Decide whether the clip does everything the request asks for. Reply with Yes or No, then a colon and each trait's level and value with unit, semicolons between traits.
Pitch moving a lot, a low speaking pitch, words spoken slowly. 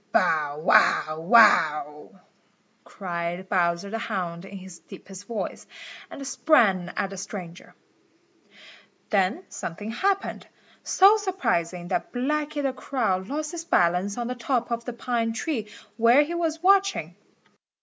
No: wide, 7.6 semitones; high, 215 Hz; slow, 130 wpm